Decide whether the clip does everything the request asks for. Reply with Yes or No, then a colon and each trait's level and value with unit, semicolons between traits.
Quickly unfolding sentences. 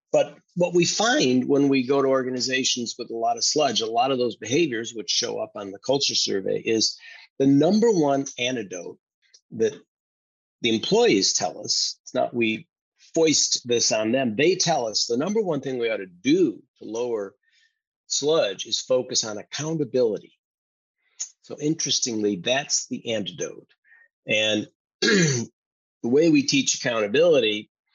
No: average, 155 wpm